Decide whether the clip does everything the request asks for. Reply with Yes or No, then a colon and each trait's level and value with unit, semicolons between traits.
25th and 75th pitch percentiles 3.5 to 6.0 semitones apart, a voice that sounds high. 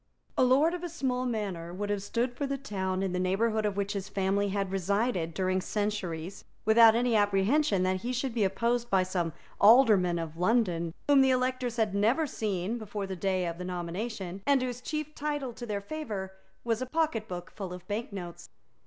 Yes: average, 4.6 semitones; high, 205 Hz